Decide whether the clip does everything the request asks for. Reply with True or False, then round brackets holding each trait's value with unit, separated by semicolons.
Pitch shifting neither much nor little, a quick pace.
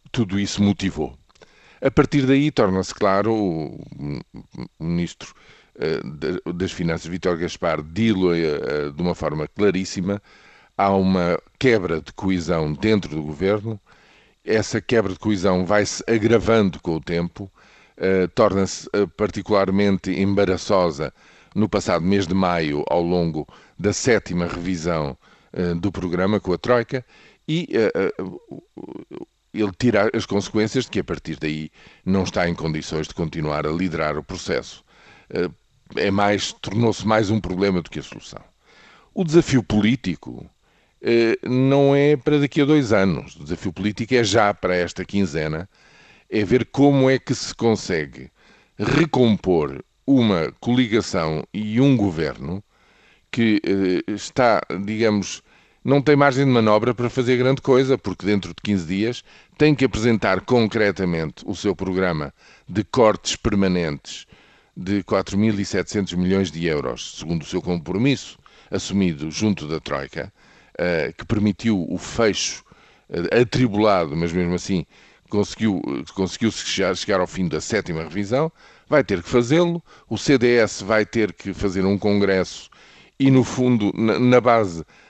False (4.6 semitones; 135 wpm)